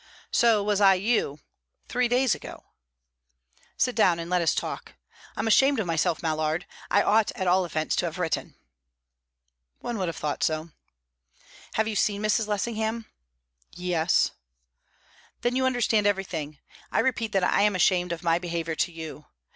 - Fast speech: No, average, 160 wpm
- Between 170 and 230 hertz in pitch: Yes, high, 190 Hz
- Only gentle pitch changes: No, average, 4.8 semitones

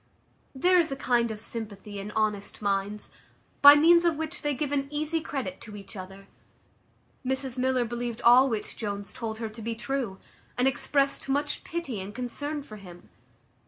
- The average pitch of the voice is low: No, high, 245 Hz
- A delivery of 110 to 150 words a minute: No, average, 175 wpm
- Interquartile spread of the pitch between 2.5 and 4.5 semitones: No, average, 5.3 semitones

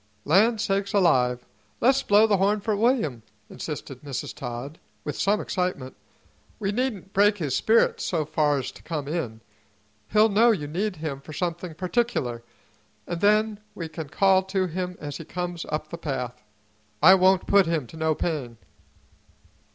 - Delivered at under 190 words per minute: Yes, average, 160 wpm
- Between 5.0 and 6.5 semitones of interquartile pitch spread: Yes, wide, 5.5 semitones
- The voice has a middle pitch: Yes, medium, 175 Hz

